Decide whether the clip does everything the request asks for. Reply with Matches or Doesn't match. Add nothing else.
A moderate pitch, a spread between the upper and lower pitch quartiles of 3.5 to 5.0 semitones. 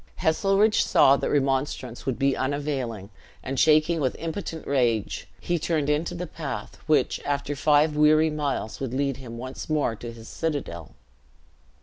Doesn't match